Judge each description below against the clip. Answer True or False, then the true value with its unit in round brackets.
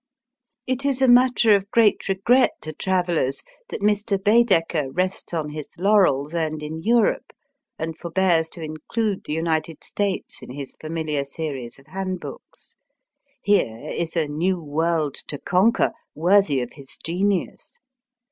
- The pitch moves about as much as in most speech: True (4.7 semitones)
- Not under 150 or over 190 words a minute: False (140 wpm)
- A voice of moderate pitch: True (170 Hz)